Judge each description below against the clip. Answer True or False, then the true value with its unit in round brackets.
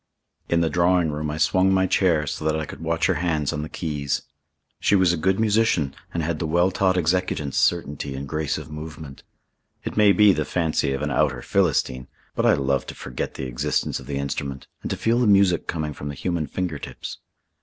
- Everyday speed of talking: False (220 wpm)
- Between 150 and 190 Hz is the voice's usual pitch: False (80 Hz)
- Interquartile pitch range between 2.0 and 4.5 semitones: True (3.9 semitones)